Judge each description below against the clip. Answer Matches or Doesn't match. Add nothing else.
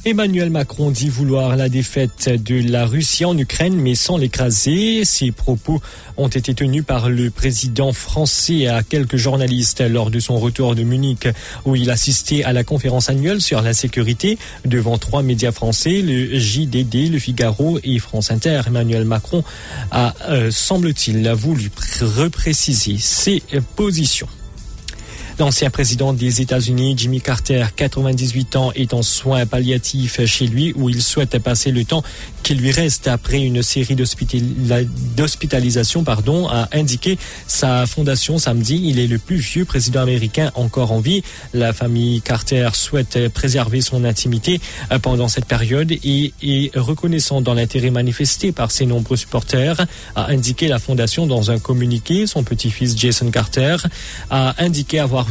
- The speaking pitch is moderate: Doesn't match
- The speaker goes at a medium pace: Matches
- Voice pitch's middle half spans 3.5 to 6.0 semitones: Doesn't match